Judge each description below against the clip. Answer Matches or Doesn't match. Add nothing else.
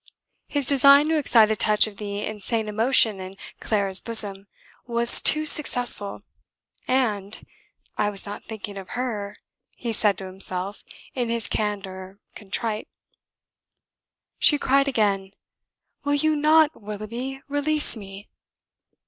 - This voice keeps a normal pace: Doesn't match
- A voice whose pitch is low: Doesn't match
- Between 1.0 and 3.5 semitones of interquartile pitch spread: Doesn't match